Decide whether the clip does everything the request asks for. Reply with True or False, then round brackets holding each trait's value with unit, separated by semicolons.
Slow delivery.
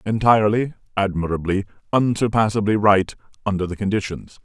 True (95 wpm)